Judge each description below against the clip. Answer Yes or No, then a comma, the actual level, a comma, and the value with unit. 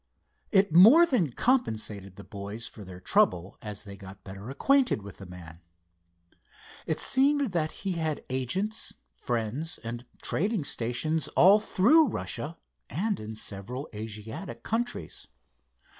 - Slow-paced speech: Yes, slow, 130 wpm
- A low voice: Yes, low, 125 Hz